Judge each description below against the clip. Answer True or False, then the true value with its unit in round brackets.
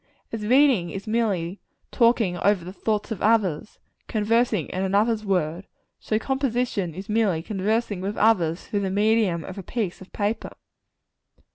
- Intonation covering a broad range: False (3.3 semitones)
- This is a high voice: True (205 Hz)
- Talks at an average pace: True (150 wpm)